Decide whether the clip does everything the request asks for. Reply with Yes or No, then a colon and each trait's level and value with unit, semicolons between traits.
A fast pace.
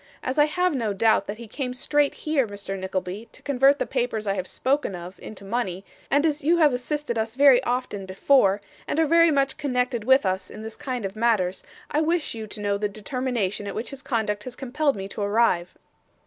Yes: fast, 220 wpm